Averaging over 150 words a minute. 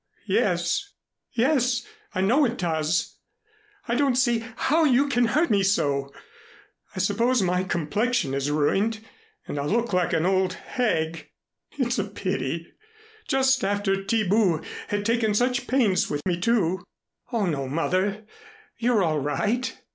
No: average, 140 wpm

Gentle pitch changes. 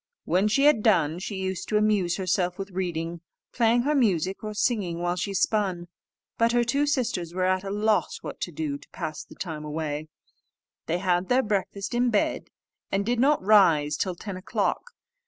No: average, 3.9 semitones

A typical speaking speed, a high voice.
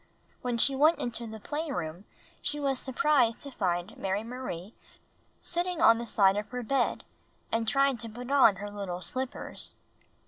Yes: average, 165 wpm; high, 235 Hz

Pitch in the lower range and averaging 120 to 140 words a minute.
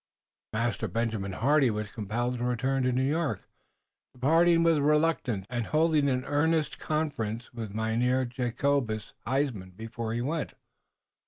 Yes: low, 125 Hz; slow, 135 wpm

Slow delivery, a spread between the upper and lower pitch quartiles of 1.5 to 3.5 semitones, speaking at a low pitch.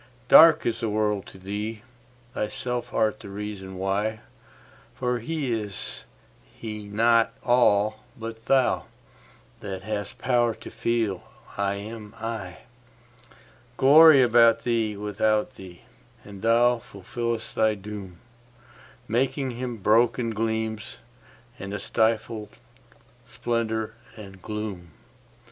Yes: slow, 100 wpm; narrow, 2.4 semitones; low, 110 Hz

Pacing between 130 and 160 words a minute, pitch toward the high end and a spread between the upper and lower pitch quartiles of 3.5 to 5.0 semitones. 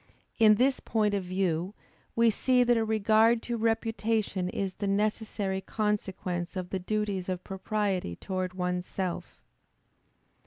No: average, 140 wpm; high, 205 Hz; average, 3.0 semitones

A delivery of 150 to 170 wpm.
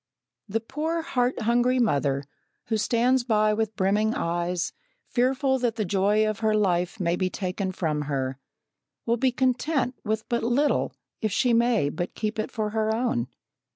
Yes: average, 165 wpm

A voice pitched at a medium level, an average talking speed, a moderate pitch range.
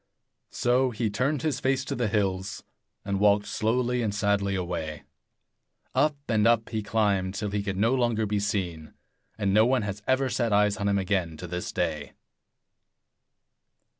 No: low, 105 Hz; average, 165 wpm; average, 3.2 semitones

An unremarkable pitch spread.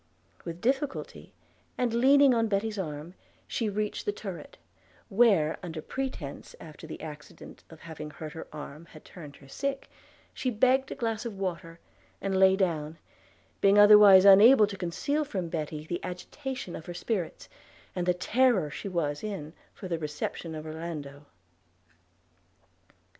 No: wide, 6.0 semitones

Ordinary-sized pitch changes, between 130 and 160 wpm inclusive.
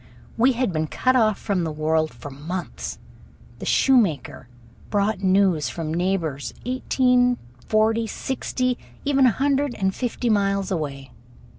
No: wide, 7.6 semitones; slow, 135 wpm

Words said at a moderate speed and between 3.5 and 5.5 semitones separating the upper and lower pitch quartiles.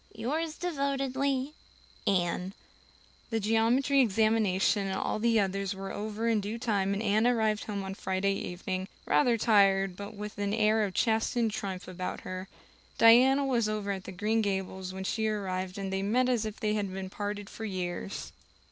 No: average, 170 wpm; average, 2.9 semitones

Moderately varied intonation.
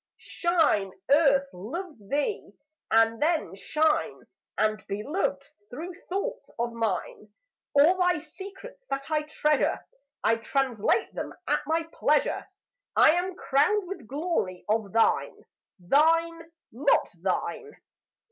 No: wide, 7.4 semitones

